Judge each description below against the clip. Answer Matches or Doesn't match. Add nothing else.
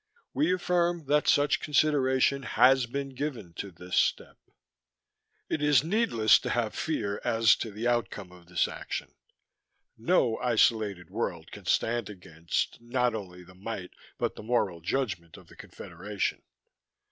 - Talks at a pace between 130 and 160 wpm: Matches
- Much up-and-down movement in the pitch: Matches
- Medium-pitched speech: Doesn't match